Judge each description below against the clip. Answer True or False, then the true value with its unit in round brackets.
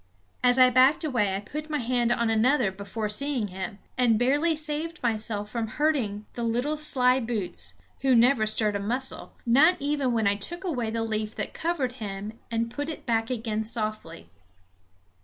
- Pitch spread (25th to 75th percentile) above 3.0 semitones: True (4.4 semitones)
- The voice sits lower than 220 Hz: False (235 Hz)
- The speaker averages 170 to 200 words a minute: True (175 wpm)